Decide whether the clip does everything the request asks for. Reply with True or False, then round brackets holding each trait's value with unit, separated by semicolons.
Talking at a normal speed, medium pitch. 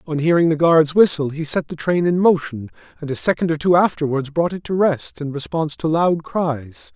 False (225 wpm; 160 Hz)